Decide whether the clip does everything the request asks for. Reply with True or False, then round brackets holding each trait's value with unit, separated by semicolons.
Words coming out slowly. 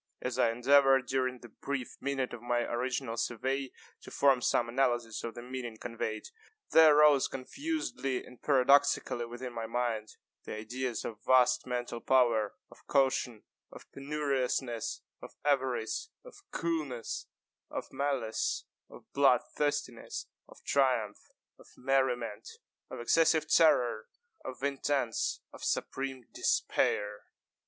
True (125 wpm)